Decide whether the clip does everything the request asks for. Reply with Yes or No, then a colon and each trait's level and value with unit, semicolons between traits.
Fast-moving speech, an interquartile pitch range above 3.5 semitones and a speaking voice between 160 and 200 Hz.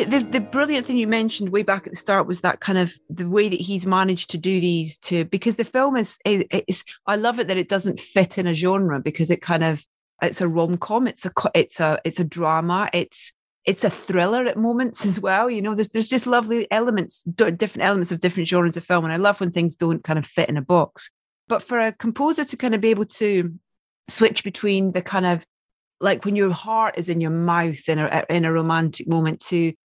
Yes: fast, 235 wpm; average, 4.3 semitones; medium, 185 Hz